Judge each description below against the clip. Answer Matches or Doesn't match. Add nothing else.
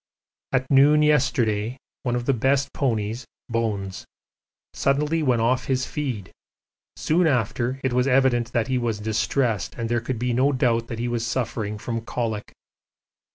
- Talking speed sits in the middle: Matches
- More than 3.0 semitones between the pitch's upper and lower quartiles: Doesn't match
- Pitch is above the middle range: Doesn't match